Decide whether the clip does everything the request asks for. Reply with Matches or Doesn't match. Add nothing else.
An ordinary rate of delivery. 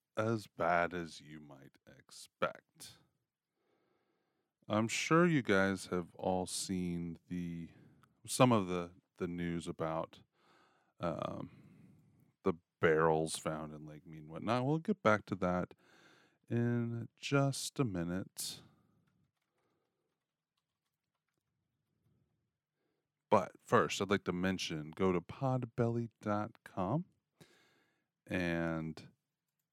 Doesn't match